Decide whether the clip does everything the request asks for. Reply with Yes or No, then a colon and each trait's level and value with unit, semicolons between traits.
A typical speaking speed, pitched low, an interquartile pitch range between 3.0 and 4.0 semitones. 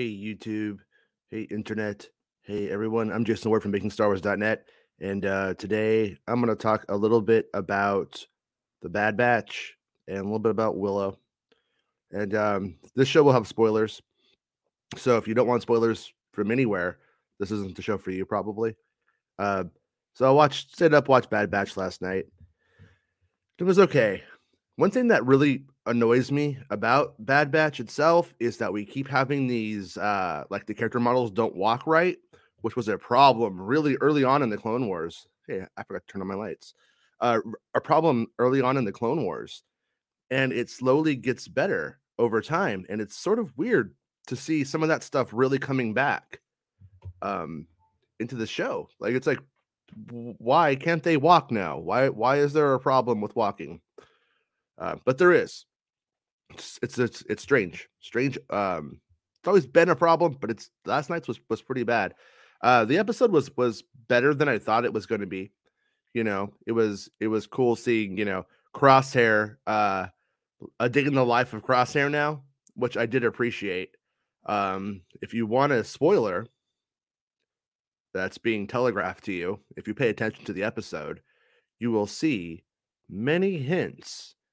No: average, 175 wpm; low, 115 Hz; average, 4.5 semitones